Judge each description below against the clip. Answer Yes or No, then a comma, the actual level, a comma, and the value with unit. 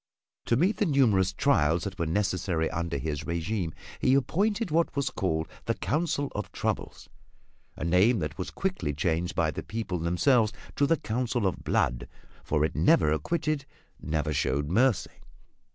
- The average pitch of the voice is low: Yes, very low, 95 Hz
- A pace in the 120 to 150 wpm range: No, average, 160 wpm